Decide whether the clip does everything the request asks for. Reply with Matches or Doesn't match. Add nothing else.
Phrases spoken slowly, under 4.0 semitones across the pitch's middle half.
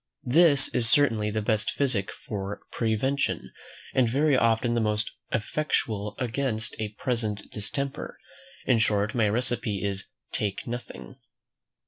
Matches